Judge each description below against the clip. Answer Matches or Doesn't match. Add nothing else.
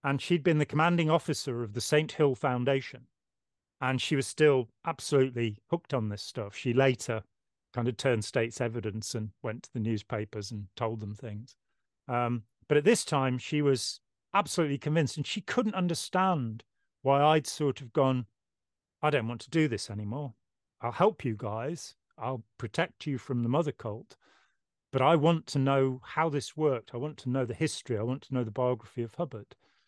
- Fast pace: Doesn't match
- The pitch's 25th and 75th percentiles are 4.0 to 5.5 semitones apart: Matches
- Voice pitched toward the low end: Matches